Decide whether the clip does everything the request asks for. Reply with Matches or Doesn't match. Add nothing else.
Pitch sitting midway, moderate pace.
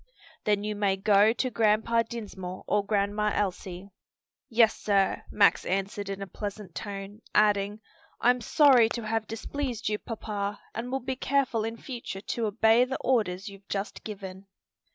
Doesn't match